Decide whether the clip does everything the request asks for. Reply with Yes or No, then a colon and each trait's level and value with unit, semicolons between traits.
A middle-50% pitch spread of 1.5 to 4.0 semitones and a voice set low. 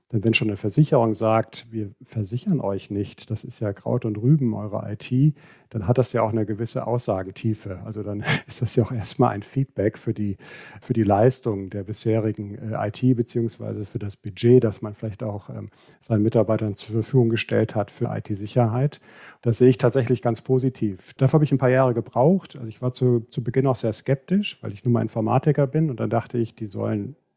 Yes: average, 2.8 semitones; low, 115 Hz